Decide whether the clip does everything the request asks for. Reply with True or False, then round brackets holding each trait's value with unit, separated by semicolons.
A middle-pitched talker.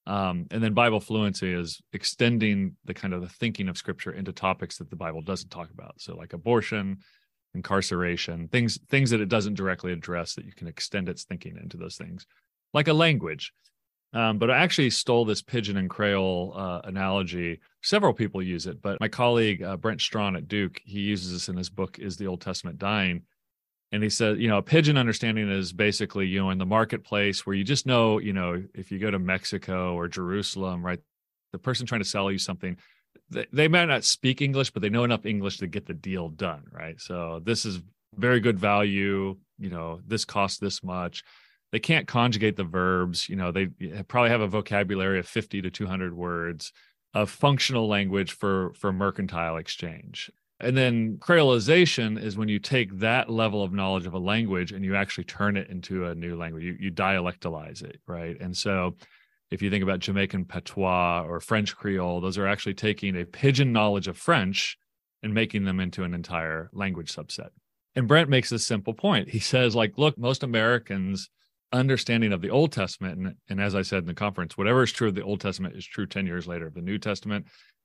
False (100 Hz)